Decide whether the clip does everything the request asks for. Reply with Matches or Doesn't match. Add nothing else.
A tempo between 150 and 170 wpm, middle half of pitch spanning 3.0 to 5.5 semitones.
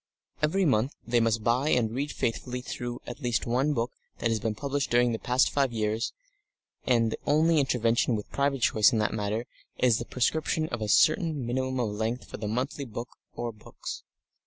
Doesn't match